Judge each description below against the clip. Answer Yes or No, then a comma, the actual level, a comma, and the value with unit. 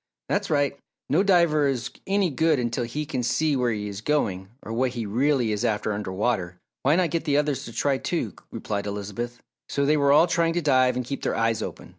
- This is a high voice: No, low, 130 Hz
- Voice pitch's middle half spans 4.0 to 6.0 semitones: Yes, average, 4.9 semitones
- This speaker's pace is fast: Yes, fast, 225 wpm